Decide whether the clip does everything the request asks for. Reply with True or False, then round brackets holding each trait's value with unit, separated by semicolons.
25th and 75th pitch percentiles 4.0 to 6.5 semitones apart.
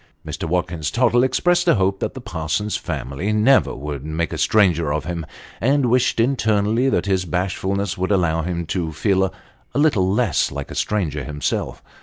True (5.3 semitones)